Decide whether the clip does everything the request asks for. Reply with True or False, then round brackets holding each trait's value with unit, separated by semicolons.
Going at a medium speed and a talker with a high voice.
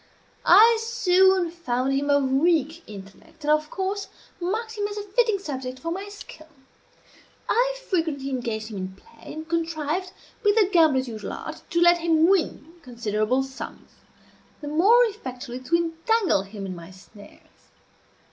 True (155 wpm; 320 Hz)